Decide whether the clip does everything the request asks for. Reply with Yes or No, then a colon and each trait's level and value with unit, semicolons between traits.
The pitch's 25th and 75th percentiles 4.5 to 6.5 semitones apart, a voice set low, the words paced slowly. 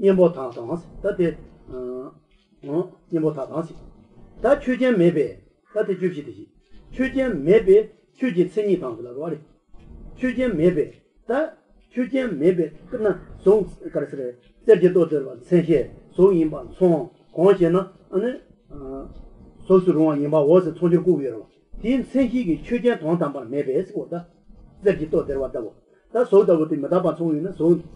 No: average, 5.1 semitones; medium, 180 Hz; slow, 105 wpm